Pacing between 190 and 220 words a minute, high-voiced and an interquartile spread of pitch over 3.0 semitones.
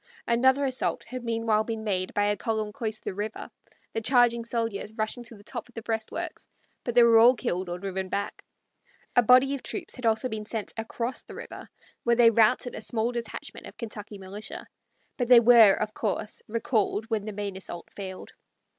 No: average, 200 wpm; high, 225 Hz; narrow, 2.4 semitones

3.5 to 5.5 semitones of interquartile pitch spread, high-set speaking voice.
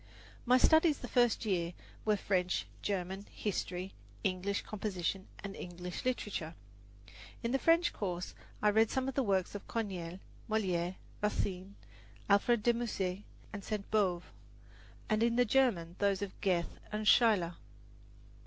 Yes: average, 3.8 semitones; high, 200 Hz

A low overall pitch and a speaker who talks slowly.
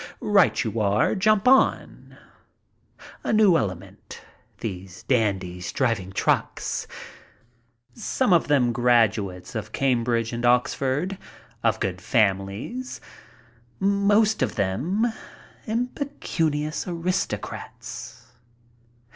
Yes: low, 125 Hz; slow, 90 wpm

